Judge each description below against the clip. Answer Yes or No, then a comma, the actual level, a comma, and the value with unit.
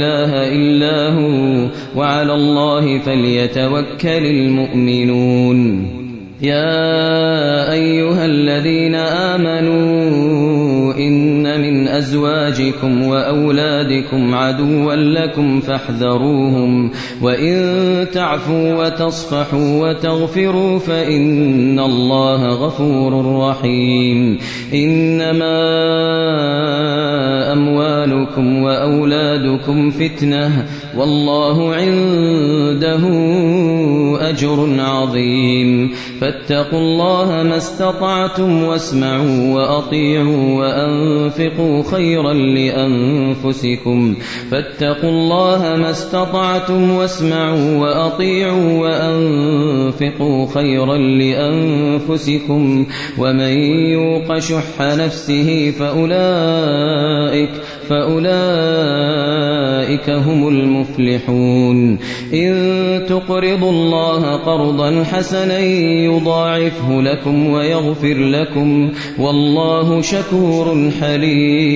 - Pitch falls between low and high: Yes, medium, 145 Hz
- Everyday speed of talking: No, slow, 55 wpm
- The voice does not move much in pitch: No, average, 3.1 semitones